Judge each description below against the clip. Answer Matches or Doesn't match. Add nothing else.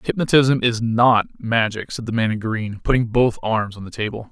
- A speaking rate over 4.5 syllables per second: Matches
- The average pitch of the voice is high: Doesn't match